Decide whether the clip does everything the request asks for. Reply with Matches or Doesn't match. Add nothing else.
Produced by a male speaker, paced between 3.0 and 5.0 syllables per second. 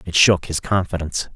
Doesn't match